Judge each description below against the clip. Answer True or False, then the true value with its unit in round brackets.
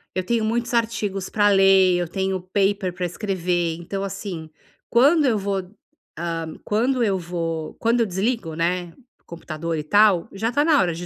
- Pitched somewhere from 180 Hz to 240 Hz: True (190 Hz)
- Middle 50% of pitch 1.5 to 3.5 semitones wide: False (4.0 semitones)